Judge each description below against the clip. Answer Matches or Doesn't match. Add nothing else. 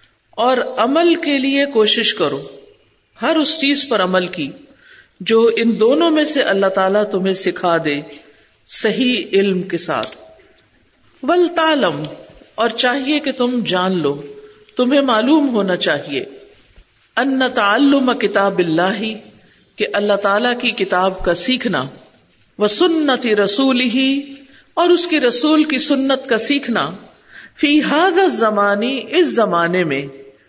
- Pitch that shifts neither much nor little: Doesn't match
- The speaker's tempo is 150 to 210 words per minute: Doesn't match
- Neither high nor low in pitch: Doesn't match